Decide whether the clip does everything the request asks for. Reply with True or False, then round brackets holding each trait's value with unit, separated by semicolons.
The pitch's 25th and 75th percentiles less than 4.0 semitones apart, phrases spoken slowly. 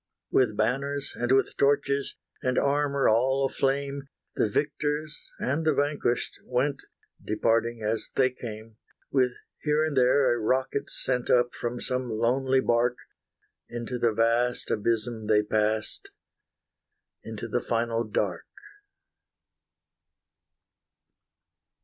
True (3.2 semitones; 115 wpm)